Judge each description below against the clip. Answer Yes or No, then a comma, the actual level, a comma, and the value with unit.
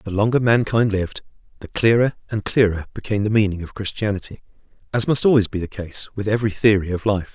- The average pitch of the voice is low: Yes, low, 105 Hz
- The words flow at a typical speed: Yes, average, 195 wpm